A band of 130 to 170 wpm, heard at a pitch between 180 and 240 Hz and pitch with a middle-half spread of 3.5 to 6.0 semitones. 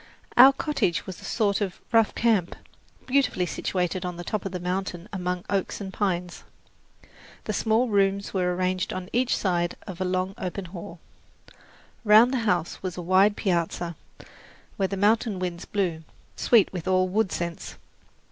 No: average, 165 wpm; medium, 185 Hz; narrow, 2.5 semitones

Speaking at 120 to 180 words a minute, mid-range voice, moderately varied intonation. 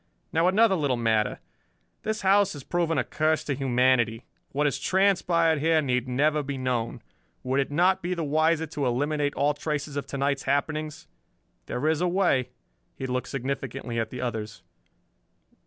Yes: average, 170 wpm; medium, 145 Hz; average, 4.0 semitones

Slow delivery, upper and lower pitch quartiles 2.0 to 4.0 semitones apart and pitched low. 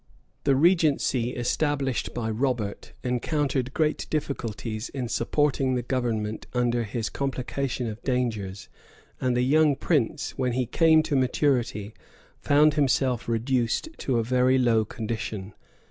Yes: slow, 130 wpm; average, 3.3 semitones; low, 125 Hz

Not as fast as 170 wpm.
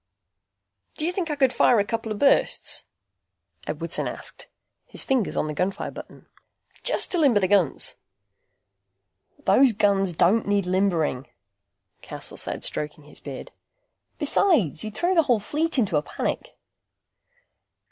Yes: average, 140 wpm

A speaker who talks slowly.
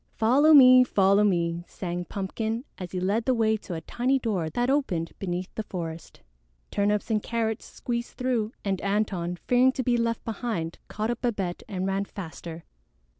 No: average, 175 wpm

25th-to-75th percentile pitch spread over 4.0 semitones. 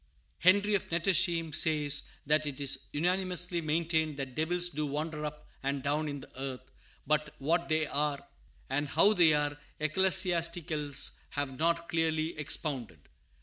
No: average, 2.7 semitones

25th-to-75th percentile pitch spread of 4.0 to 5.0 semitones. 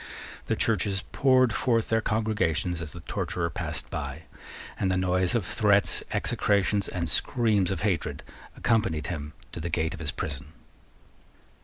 Yes: average, 4.4 semitones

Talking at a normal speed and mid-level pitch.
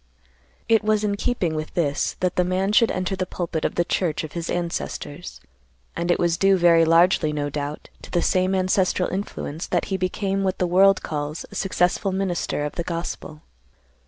Yes: average, 190 wpm; medium, 180 Hz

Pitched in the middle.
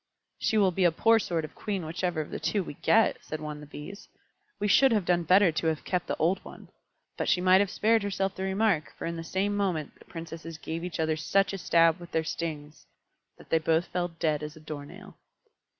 Yes: medium, 175 Hz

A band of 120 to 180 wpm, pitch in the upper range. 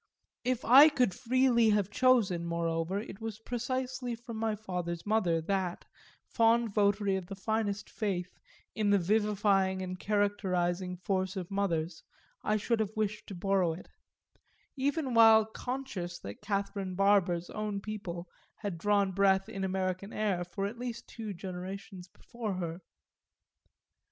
Yes: average, 140 wpm; high, 200 Hz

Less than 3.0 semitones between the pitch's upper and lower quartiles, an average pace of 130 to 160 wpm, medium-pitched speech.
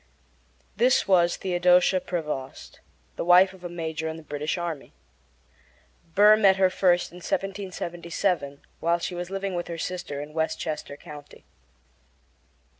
Yes: narrow, 2.6 semitones; slow, 135 wpm; medium, 175 Hz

